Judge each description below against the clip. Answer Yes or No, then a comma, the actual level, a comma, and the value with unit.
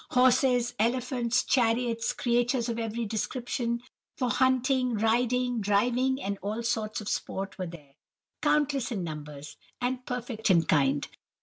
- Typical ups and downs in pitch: Yes, average, 3.3 semitones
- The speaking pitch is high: Yes, high, 235 Hz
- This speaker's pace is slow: Yes, slow, 130 wpm